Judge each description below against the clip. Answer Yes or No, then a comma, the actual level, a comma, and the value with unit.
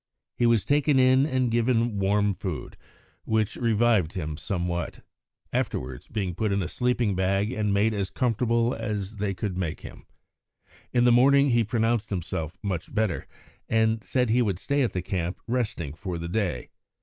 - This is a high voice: No, low, 110 Hz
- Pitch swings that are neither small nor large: Yes, average, 4.0 semitones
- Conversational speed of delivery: Yes, average, 170 wpm